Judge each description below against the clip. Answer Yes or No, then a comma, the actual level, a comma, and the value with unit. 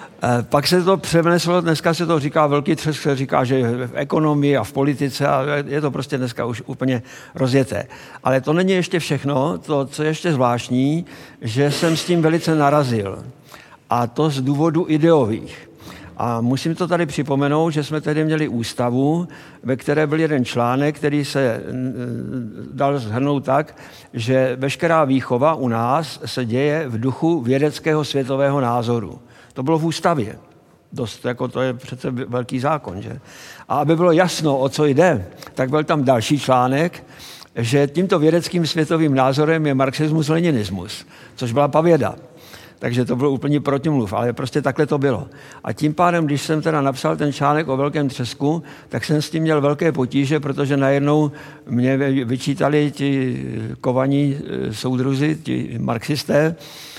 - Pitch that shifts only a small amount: No, average, 3.2 semitones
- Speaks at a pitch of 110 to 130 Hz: No, medium, 140 Hz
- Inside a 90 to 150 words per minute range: No, average, 160 wpm